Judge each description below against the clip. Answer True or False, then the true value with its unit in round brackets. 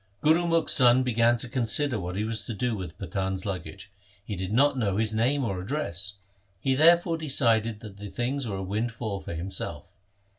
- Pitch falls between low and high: False (110 Hz)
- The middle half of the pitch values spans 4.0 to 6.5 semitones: True (5.1 semitones)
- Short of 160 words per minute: False (200 wpm)